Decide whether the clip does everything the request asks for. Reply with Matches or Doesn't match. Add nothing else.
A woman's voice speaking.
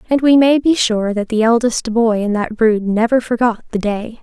Matches